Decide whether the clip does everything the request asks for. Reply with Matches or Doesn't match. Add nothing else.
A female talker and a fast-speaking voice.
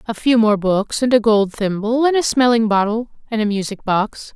Matches